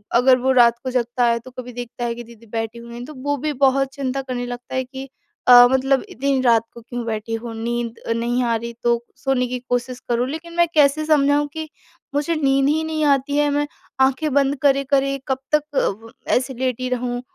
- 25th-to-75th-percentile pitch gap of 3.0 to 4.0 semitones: No, narrow, 2.6 semitones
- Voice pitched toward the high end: Yes, very high, 255 Hz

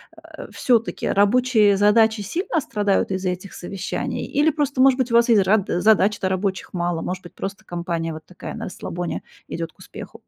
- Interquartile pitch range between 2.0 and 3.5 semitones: No, average, 4.4 semitones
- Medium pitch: No, high, 200 Hz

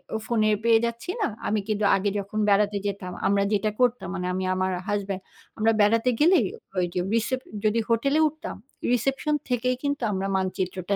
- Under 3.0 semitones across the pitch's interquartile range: No, average, 4.0 semitones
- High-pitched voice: Yes, high, 215 Hz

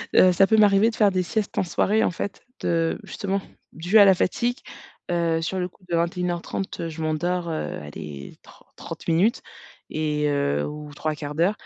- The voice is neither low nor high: Yes, medium, 175 Hz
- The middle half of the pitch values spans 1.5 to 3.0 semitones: No, average, 3.8 semitones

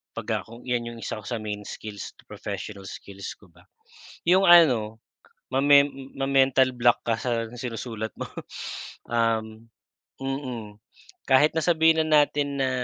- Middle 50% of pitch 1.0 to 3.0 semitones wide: No, average, 3.8 semitones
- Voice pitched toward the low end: Yes, low, 120 Hz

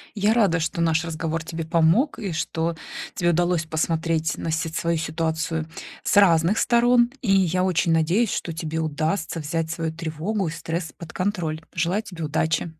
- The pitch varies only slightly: Yes, narrow, 2.2 semitones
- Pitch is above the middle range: No, medium, 165 Hz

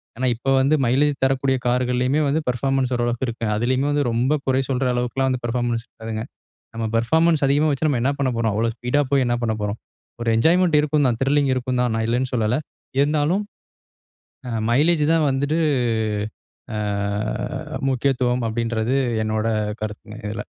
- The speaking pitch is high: No, low, 125 Hz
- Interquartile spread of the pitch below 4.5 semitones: Yes, average, 3.2 semitones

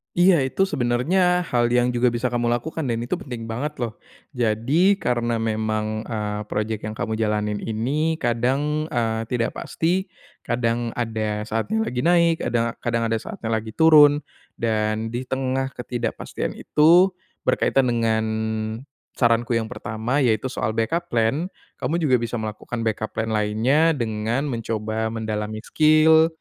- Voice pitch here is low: Yes, low, 120 Hz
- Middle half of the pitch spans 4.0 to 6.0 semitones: Yes, average, 4.3 semitones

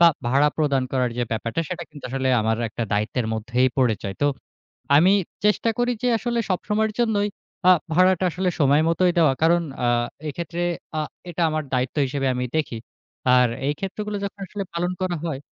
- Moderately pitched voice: Yes, medium, 155 Hz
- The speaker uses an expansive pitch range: Yes, wide, 6.2 semitones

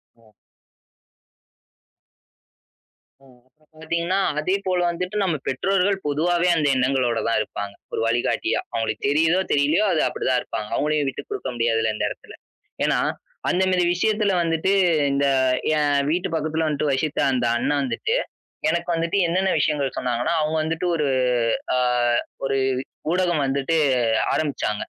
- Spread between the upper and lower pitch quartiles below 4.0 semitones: No, average, 4.7 semitones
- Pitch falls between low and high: Yes, medium, 155 Hz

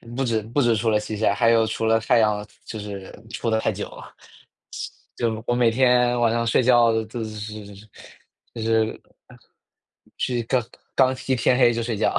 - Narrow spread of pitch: Yes, narrow, 1.8 semitones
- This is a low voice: Yes, low, 115 Hz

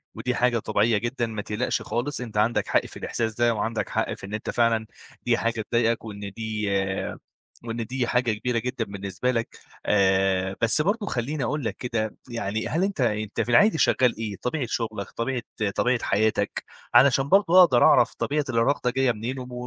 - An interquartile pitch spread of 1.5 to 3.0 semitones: Yes, average, 2.7 semitones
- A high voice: No, low, 115 Hz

